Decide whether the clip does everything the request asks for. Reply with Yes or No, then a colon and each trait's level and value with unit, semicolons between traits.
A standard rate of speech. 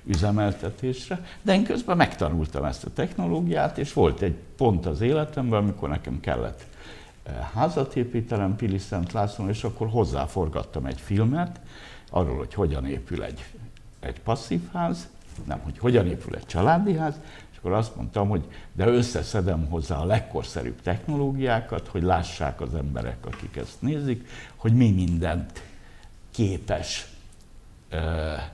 Yes: average, 135 wpm